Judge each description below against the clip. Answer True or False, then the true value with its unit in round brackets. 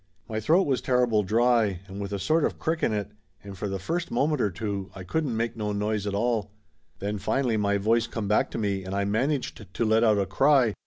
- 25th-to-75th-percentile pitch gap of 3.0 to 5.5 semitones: True (3.4 semitones)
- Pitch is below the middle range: True (110 Hz)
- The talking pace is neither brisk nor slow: False (235 wpm)